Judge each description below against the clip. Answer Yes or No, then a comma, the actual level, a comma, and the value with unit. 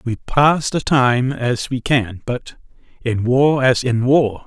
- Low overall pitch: Yes, low, 125 Hz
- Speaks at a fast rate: No, average, 175 wpm